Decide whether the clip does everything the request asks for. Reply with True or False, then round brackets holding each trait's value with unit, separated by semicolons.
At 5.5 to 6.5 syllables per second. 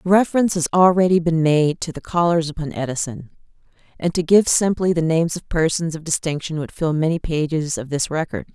True (5.7 syllables/s)